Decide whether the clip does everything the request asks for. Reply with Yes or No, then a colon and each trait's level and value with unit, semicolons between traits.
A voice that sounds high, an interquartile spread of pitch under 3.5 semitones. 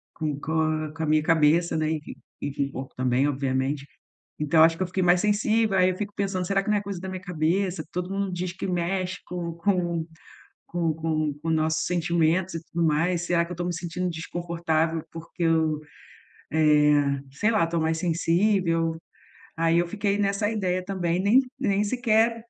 No: medium, 170 Hz; average, 2.8 semitones